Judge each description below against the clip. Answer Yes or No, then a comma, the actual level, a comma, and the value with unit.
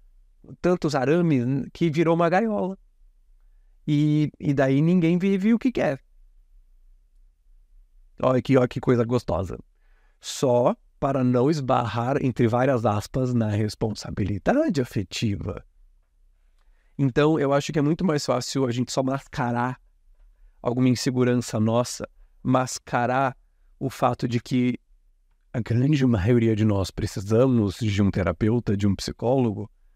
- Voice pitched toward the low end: Yes, low, 120 Hz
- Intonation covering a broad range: Yes, wide, 5.9 semitones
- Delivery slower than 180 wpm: Yes, average, 125 wpm